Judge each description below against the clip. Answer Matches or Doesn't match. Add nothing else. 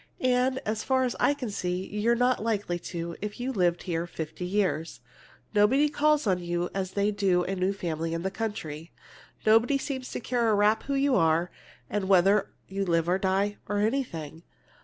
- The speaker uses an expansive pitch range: Doesn't match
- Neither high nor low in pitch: Doesn't match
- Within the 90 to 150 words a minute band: Doesn't match